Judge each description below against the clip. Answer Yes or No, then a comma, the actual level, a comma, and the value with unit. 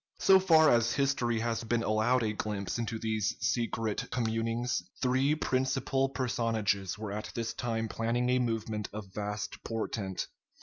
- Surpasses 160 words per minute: No, average, 145 wpm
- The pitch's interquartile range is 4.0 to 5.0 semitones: No, narrow, 2.5 semitones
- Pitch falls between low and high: No, low, 115 Hz